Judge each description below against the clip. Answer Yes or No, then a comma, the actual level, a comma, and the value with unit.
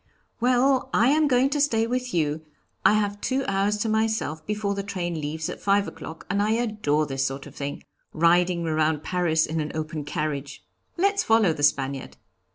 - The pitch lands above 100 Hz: Yes, medium, 185 Hz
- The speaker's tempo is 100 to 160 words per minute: No, average, 185 wpm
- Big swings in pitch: Yes, wide, 6.4 semitones